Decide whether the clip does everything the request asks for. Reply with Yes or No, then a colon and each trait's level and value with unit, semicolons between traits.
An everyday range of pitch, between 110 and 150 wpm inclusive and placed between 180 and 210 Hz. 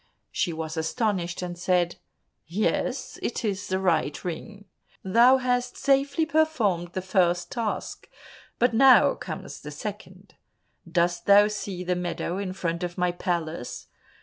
Yes: average, 4.7 semitones; average, 140 wpm; medium, 185 Hz